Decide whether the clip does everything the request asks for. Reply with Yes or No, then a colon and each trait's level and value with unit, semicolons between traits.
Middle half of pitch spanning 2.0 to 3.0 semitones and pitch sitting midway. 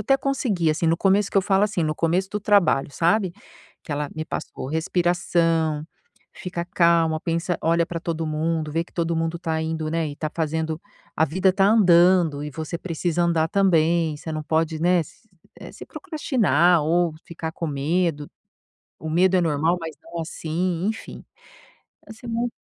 Yes: narrow, 2.4 semitones; medium, 165 Hz